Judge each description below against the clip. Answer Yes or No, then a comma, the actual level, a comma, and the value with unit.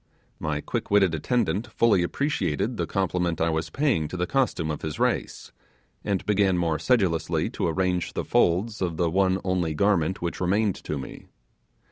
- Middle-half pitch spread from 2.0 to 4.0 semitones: Yes, average, 3.6 semitones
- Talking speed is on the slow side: No, average, 170 wpm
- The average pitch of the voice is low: Yes, very low, 90 Hz